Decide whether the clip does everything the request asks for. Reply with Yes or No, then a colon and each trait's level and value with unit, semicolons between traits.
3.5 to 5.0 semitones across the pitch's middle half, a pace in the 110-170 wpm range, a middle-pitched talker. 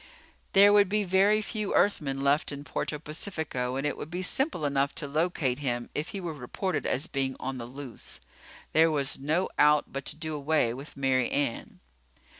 No: average, 4.6 semitones; average, 190 wpm; medium, 150 Hz